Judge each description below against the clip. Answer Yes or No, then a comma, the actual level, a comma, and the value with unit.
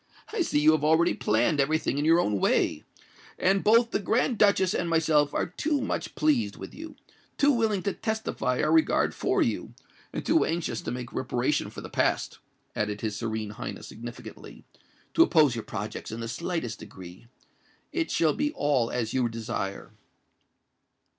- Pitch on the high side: No, medium, 150 Hz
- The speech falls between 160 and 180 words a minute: Yes, average, 175 wpm